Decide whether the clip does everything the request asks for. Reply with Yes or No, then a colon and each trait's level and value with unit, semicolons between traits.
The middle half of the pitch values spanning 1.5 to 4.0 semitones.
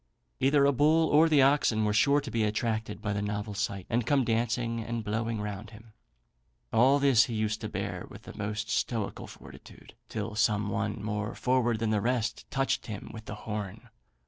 Yes: average, 2.8 semitones